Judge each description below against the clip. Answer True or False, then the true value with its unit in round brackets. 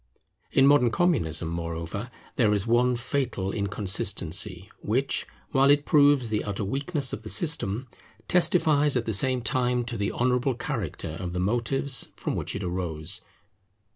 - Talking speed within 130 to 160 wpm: True (150 wpm)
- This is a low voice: True (115 Hz)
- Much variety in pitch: True (5.7 semitones)